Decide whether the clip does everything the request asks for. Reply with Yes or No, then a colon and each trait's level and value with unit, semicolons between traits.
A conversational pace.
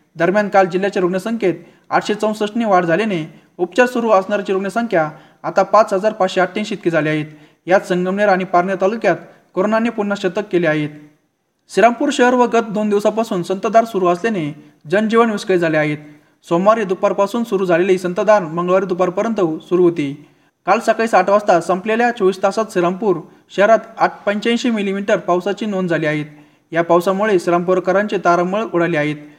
No: fast, 150 wpm